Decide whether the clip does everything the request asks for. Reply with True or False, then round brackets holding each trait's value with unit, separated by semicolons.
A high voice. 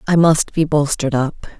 False (150 Hz)